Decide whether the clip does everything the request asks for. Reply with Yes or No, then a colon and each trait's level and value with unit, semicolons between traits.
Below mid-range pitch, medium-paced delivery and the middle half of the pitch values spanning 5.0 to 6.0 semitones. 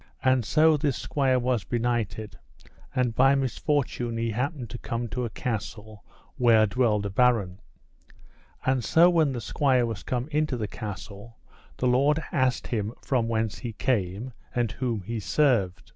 No: low, 120 Hz; average, 160 wpm; average, 3.2 semitones